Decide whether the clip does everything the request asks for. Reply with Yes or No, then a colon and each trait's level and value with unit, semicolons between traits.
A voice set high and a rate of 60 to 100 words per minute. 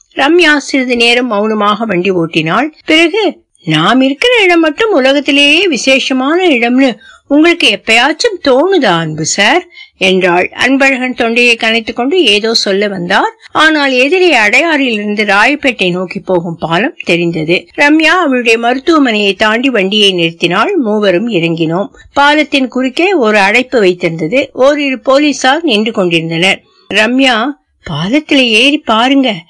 No: very high, 250 Hz; average, 115 wpm